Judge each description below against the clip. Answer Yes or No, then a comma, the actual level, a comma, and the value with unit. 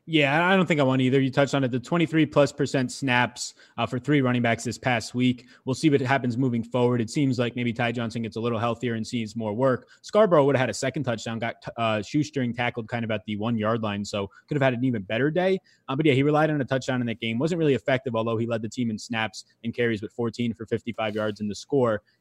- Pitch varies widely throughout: No, average, 3.1 semitones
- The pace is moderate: No, fast, 275 wpm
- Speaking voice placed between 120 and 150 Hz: Yes, low, 125 Hz